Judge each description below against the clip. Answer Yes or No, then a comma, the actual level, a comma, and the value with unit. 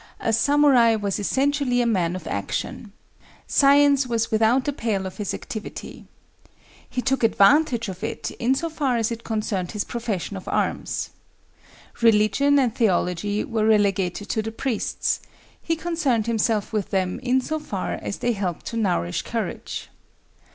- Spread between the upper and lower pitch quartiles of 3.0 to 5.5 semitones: Yes, average, 4.4 semitones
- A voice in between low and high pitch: No, high, 225 Hz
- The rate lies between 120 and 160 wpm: Yes, average, 155 wpm